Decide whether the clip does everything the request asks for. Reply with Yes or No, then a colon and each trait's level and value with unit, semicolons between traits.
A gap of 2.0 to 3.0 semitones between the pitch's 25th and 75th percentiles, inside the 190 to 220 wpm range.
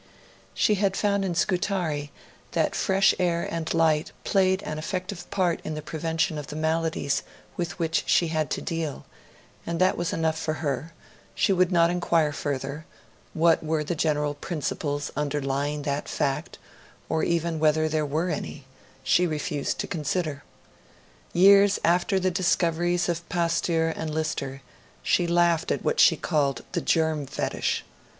No: narrow, 2.6 semitones; average, 155 wpm